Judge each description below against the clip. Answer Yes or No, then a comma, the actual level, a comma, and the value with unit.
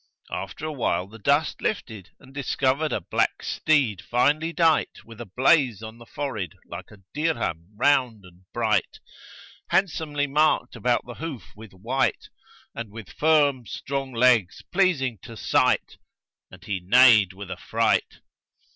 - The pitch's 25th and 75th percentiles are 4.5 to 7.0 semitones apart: Yes, wide, 5.6 semitones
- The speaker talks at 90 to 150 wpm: Yes, average, 145 wpm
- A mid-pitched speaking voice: No, low, 125 Hz